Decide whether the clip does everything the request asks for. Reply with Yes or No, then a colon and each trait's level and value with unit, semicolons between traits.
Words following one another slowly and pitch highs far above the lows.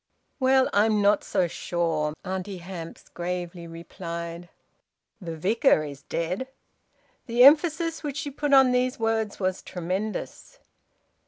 Yes: slow, 120 wpm; wide, 6.6 semitones